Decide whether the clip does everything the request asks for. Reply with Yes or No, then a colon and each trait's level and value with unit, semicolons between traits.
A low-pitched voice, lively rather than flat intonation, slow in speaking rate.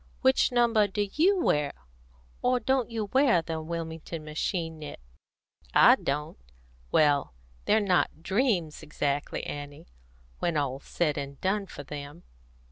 No: medium, 165 Hz; wide, 6.6 semitones; slow, 130 wpm